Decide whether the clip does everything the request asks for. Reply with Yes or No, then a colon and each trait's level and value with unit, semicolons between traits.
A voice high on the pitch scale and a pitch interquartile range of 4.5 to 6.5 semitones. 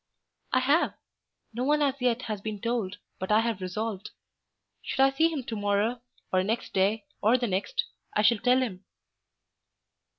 No: high, 230 Hz; average, 3.9 semitones